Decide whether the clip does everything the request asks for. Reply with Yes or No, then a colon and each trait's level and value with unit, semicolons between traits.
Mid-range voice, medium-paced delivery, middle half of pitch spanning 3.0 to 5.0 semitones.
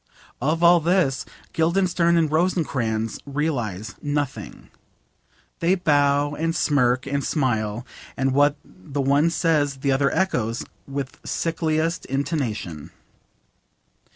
No: medium, 145 Hz; slow, 105 wpm; average, 4.0 semitones